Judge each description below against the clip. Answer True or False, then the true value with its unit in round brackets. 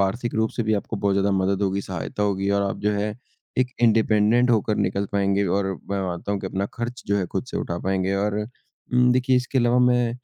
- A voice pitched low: True (100 Hz)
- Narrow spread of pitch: False (3.3 semitones)